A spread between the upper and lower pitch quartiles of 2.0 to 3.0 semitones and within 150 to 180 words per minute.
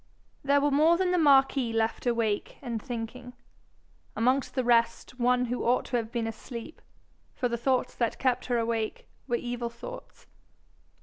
Yes: narrow, 2.5 semitones; average, 165 wpm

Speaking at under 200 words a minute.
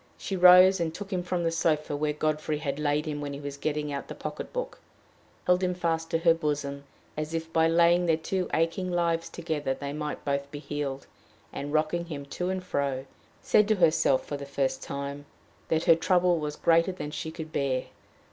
No: fast, 205 wpm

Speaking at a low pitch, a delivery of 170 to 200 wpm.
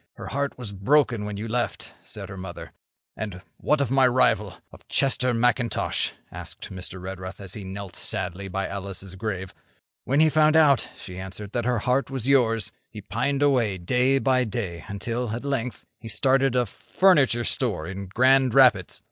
Yes: low, 115 Hz; average, 175 wpm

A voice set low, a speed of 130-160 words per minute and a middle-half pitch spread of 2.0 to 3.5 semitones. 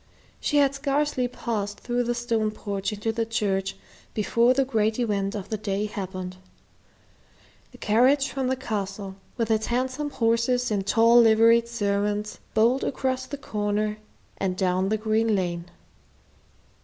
No: high, 220 Hz; average, 145 wpm; average, 3.1 semitones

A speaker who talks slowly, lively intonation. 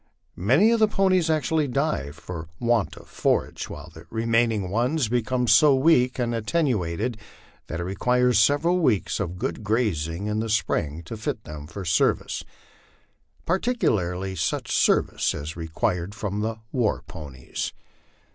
No: average, 150 wpm; wide, 6.4 semitones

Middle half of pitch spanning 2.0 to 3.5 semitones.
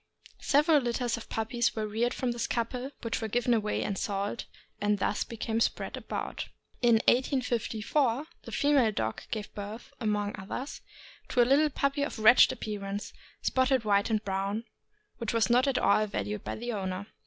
Yes: average, 3.2 semitones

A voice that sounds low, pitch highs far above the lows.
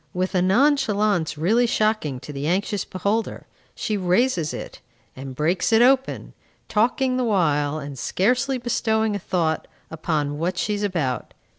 No: high, 190 Hz; wide, 6.0 semitones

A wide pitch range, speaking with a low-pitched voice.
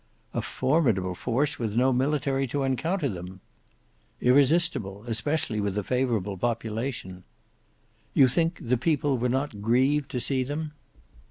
No: average, 4.5 semitones; low, 125 Hz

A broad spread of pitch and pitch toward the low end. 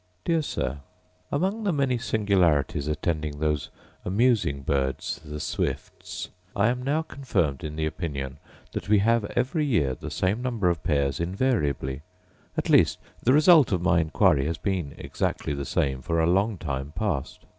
Yes: wide, 8.3 semitones; very low, 85 Hz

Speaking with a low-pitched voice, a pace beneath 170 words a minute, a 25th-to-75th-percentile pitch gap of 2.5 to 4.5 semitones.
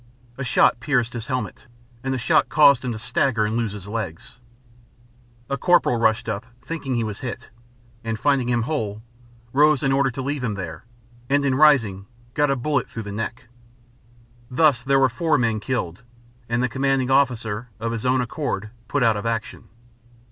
No: low, 125 Hz; average, 185 wpm; average, 3.3 semitones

